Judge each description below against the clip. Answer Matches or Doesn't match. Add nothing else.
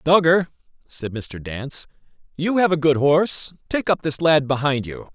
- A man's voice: Matches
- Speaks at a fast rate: Doesn't match